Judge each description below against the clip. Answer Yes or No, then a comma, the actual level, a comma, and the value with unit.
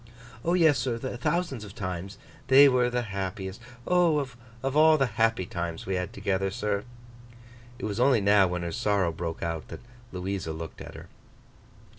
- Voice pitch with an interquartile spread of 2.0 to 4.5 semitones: No, wide, 5.5 semitones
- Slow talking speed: No, average, 165 wpm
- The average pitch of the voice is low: Yes, low, 105 Hz